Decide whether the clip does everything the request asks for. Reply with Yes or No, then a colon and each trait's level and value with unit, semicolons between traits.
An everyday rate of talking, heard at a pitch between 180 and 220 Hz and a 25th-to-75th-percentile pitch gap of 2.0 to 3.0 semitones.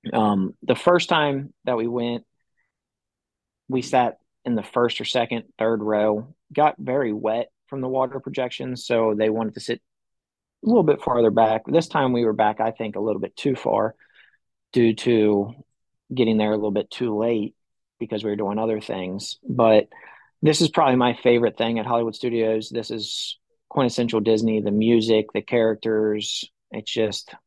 No: average, 175 wpm; low, 115 Hz; narrow, 2.6 semitones